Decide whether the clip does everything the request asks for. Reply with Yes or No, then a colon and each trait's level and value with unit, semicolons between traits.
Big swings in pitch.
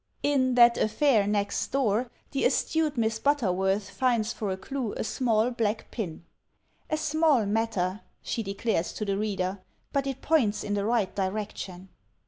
No: average, 4.4 semitones